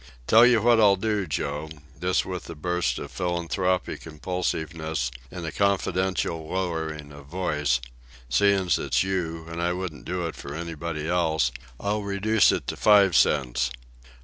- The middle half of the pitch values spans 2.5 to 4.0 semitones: Yes, average, 3.3 semitones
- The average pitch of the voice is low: Yes, very low, 85 Hz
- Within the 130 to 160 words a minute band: Yes, average, 150 wpm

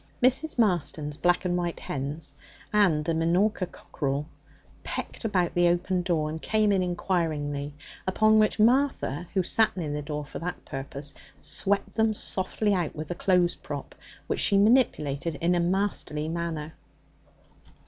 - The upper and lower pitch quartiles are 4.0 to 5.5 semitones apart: Yes, average, 4.8 semitones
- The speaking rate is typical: Yes, average, 150 wpm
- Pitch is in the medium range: Yes, medium, 175 Hz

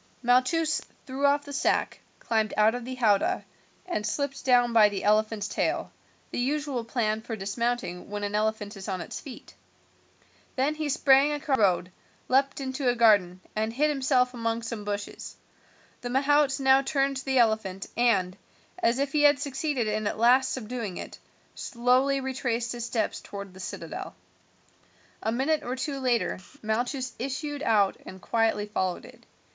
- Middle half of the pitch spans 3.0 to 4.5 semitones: Yes, average, 4.1 semitones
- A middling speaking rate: Yes, average, 165 wpm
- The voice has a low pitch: No, high, 245 Hz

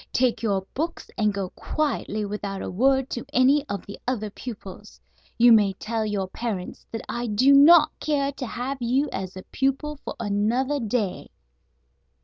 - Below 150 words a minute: No, average, 165 wpm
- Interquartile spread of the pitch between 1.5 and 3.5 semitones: No, average, 4.8 semitones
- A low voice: No, high, 235 Hz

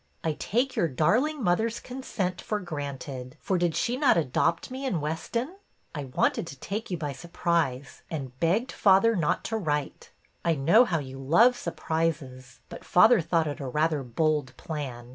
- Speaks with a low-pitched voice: No, medium, 165 Hz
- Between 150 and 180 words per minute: Yes, average, 170 wpm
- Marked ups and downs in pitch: Yes, wide, 6.8 semitones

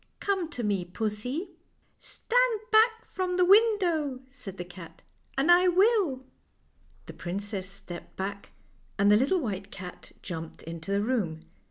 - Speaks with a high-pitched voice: Yes, high, 245 Hz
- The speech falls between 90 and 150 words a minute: No, average, 160 wpm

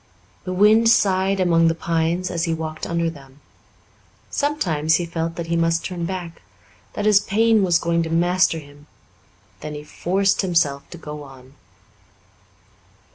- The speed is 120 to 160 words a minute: Yes, average, 155 wpm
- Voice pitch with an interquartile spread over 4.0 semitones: No, narrow, 2.6 semitones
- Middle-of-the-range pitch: Yes, medium, 170 Hz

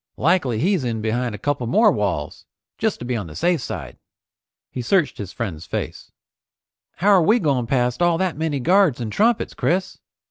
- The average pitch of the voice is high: No, medium, 140 Hz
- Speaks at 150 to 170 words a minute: No, average, 185 wpm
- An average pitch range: No, wide, 7.4 semitones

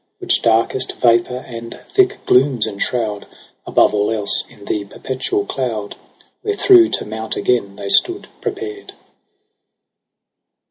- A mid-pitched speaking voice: No, low, 120 Hz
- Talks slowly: Yes, slow, 120 wpm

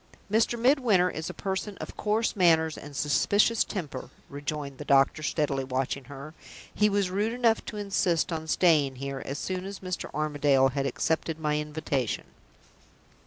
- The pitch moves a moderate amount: No, wide, 5.7 semitones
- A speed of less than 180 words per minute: Yes, average, 160 wpm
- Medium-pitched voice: Yes, medium, 160 Hz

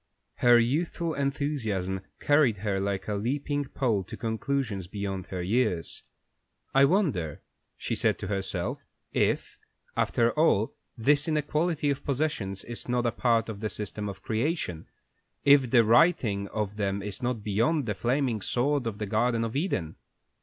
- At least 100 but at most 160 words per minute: Yes, average, 155 wpm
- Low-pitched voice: Yes, low, 115 Hz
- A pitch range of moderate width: No, wide, 5.7 semitones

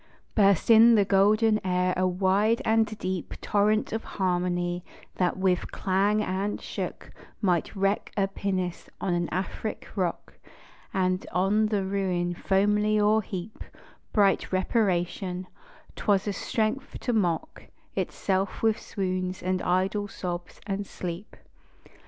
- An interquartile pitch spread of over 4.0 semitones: No, narrow, 2.4 semitones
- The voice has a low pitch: No, high, 195 Hz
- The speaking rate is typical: No, slow, 125 wpm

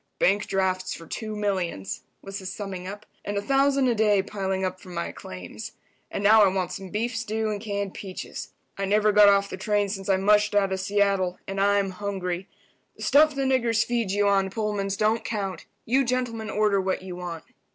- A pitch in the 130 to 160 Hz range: No, high, 200 Hz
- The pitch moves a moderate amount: No, narrow, 2.1 semitones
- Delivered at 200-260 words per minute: Yes, fast, 205 wpm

